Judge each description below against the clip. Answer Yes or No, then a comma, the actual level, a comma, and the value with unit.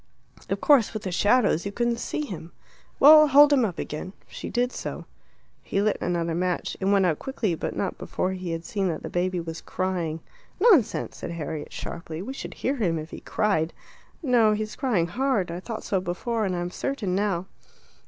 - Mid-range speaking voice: No, high, 195 Hz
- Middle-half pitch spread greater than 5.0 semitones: Yes, wide, 5.5 semitones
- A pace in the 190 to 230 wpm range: Yes, average, 195 wpm